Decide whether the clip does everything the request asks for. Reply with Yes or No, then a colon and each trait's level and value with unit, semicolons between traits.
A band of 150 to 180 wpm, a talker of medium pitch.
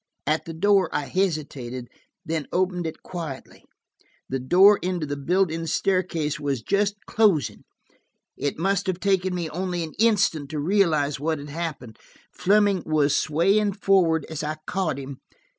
Yes: average, 155 wpm; medium, 165 Hz